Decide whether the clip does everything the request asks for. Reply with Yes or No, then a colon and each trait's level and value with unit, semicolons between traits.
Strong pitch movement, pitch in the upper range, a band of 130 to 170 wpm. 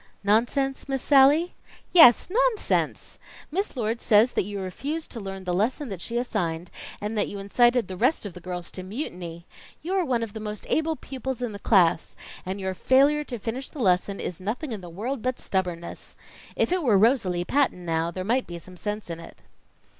No: wide, 6.2 semitones; high, 215 Hz; average, 200 wpm